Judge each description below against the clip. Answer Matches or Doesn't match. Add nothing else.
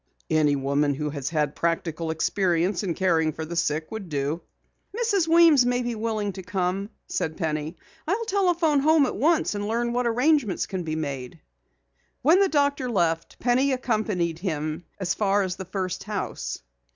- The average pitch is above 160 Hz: Matches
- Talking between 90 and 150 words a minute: Doesn't match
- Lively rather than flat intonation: Matches